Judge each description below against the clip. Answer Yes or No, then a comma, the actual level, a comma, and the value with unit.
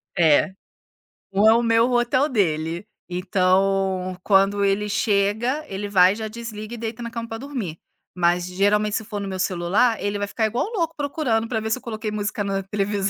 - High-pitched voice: Yes, high, 205 Hz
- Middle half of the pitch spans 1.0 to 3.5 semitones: Yes, average, 2.9 semitones